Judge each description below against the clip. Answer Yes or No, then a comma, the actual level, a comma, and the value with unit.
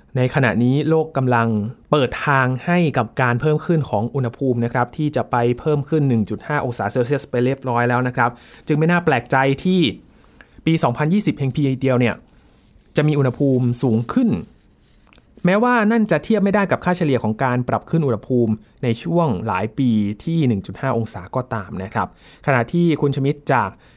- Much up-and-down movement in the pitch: No, average, 4.5 semitones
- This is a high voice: No, low, 130 Hz